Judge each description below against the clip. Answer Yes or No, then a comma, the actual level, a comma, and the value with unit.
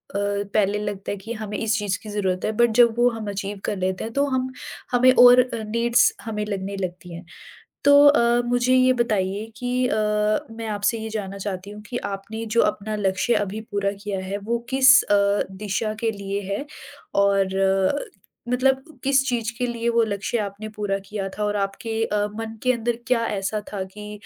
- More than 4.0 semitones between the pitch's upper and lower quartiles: No, average, 3.1 semitones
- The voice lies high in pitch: Yes, high, 210 Hz